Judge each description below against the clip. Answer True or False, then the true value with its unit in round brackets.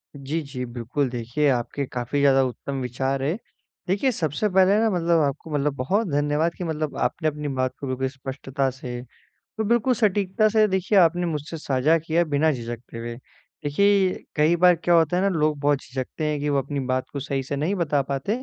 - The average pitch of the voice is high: False (150 Hz)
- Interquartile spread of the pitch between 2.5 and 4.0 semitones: False (4.6 semitones)